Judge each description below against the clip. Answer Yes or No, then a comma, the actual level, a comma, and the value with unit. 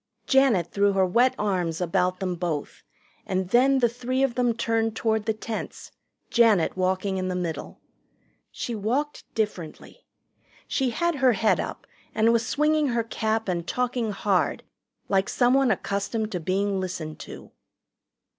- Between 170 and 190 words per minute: No, average, 150 wpm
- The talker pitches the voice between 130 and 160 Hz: No, high, 220 Hz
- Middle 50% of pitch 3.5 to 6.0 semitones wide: Yes, average, 4.6 semitones